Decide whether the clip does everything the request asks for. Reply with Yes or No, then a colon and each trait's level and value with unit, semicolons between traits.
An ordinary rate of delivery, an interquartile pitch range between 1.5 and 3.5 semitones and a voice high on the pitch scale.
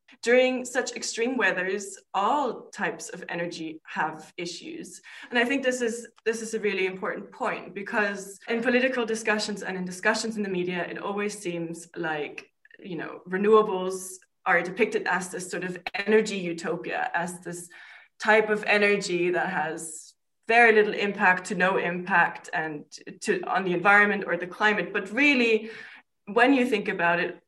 No: average, 160 wpm; average, 3.9 semitones; high, 205 Hz